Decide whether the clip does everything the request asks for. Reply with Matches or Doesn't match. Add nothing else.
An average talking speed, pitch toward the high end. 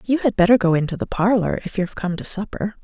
Doesn't match